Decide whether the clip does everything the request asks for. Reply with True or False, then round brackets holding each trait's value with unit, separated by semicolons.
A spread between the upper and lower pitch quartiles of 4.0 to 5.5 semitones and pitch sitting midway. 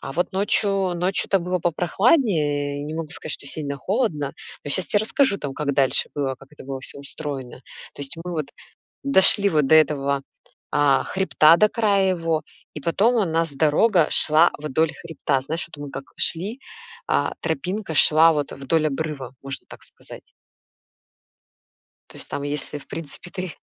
True (4.6 semitones; 160 Hz)